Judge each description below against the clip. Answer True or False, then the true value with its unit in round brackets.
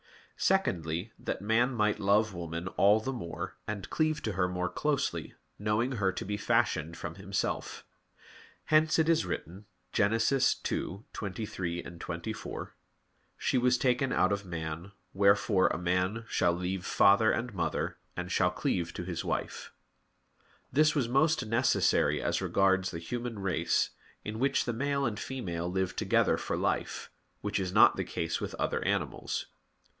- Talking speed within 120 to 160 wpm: True (150 wpm)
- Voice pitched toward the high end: False (100 Hz)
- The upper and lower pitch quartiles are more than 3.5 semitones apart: True (5.0 semitones)